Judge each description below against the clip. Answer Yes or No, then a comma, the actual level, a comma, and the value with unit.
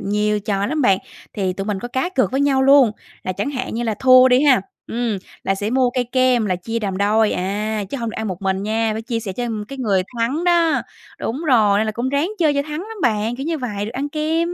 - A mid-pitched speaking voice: No, high, 235 Hz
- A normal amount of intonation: Yes, average, 4.7 semitones